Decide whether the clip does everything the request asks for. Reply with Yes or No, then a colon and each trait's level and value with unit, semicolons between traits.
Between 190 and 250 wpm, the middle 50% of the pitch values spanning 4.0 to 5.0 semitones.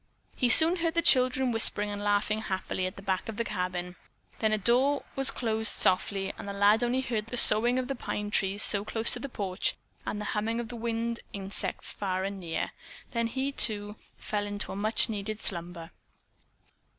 No: average, 195 wpm; average, 3.2 semitones